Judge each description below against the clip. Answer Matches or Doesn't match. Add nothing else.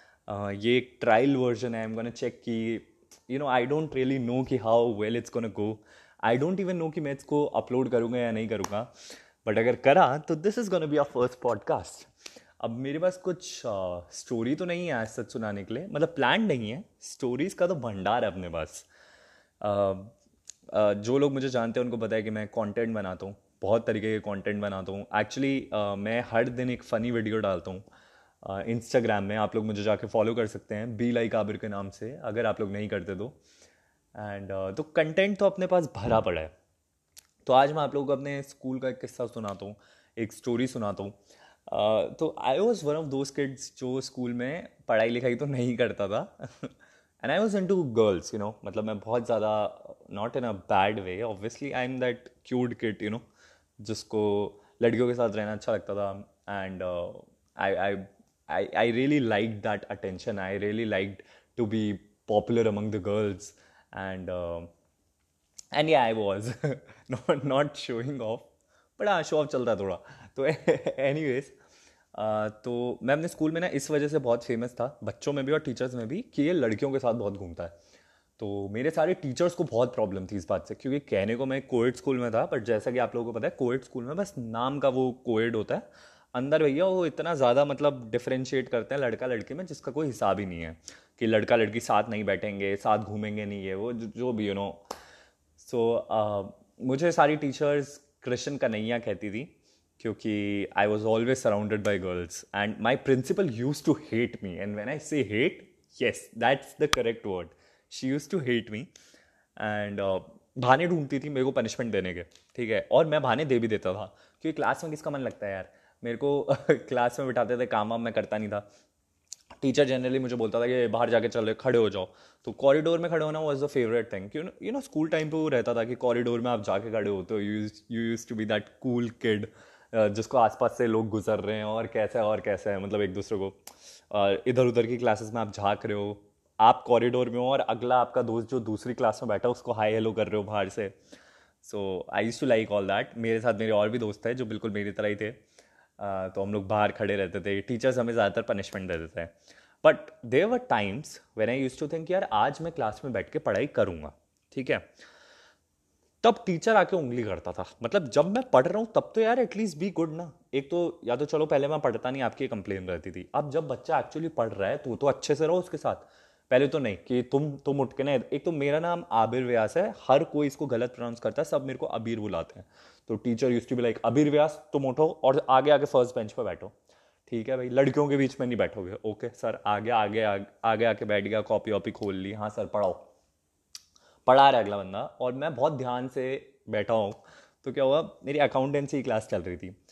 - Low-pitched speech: Matches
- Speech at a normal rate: Doesn't match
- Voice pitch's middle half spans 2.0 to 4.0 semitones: Doesn't match